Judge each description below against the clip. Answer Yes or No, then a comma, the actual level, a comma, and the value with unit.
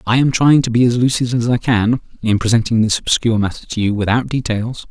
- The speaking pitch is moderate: No, low, 115 Hz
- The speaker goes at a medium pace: No, fast, 230 wpm